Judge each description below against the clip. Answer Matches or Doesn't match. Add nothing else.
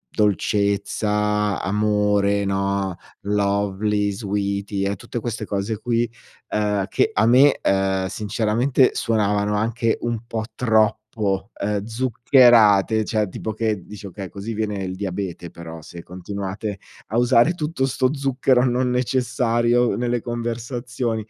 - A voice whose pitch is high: Doesn't match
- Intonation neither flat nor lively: Matches